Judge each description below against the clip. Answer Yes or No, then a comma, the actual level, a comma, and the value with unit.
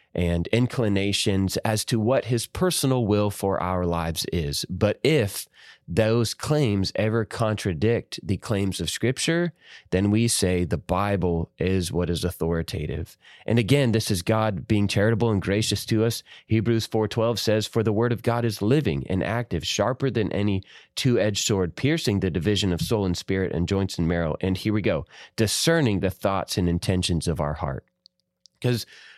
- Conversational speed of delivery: Yes, average, 170 wpm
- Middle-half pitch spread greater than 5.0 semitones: No, average, 4.0 semitones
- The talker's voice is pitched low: Yes, low, 105 Hz